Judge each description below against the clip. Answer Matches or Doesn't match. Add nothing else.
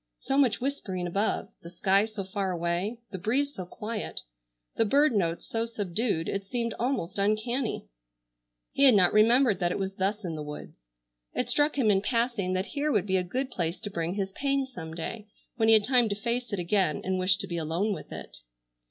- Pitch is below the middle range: Doesn't match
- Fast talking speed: Matches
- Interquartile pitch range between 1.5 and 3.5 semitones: Doesn't match